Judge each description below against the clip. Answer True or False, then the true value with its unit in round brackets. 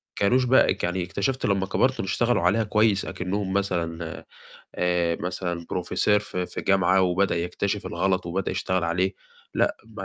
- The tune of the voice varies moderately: False (2.3 semitones)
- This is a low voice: True (95 Hz)